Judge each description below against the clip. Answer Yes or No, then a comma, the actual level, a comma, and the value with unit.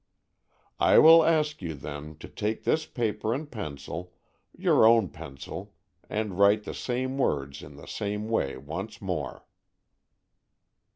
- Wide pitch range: Yes, wide, 7.6 semitones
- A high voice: No, low, 105 Hz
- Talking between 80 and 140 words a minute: Yes, slow, 135 wpm